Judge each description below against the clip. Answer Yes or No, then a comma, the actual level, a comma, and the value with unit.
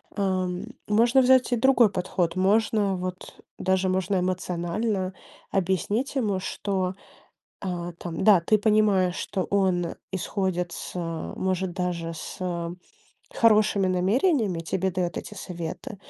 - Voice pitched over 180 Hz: Yes, high, 190 Hz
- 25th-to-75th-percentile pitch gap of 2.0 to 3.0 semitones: Yes, average, 2.7 semitones